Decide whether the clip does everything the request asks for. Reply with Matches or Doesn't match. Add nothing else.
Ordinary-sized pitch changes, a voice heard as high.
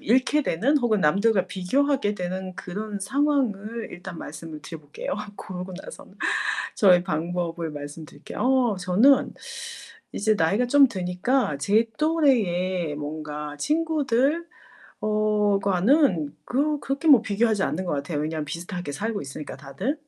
Doesn't match